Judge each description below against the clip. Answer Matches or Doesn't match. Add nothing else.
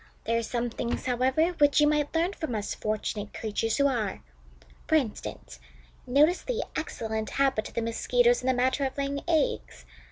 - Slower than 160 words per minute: Doesn't match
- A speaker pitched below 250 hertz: Doesn't match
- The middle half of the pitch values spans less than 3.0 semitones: Doesn't match